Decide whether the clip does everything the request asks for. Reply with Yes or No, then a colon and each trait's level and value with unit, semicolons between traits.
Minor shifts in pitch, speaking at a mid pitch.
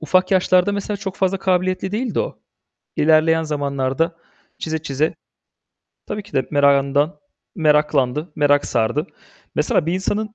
No: average, 4.5 semitones; medium, 160 Hz